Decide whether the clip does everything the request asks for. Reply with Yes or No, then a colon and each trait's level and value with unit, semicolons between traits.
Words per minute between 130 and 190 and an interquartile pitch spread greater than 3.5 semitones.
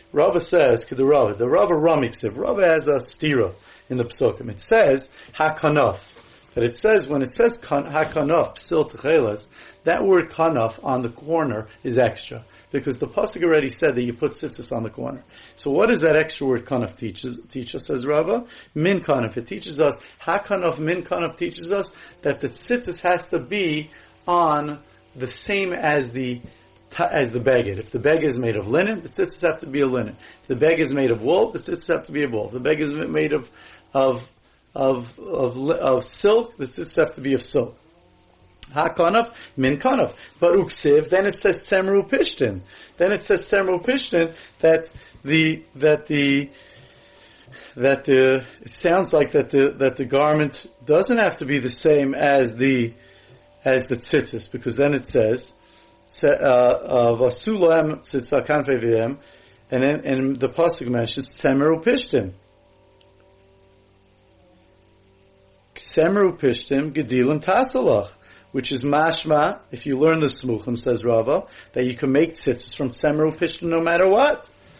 Yes: average, 160 wpm; average, 4.9 semitones